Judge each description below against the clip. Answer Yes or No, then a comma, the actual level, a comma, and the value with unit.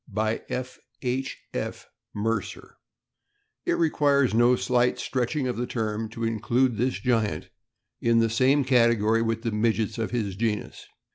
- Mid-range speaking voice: No, low, 115 Hz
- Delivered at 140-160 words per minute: Yes, average, 145 wpm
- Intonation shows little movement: Yes, narrow, 2.2 semitones